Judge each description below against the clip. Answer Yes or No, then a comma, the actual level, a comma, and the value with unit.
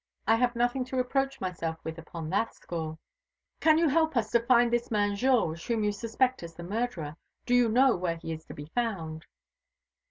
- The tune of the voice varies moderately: No, wide, 6.7 semitones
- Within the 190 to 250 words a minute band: Yes, average, 200 wpm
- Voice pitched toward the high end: Yes, high, 225 Hz